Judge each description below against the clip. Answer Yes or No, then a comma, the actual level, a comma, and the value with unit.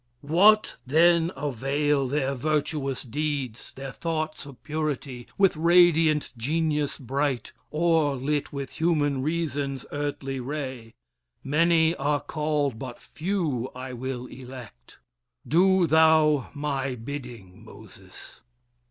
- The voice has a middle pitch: Yes, medium, 145 Hz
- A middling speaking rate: No, slow, 110 wpm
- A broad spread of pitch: No, average, 3.2 semitones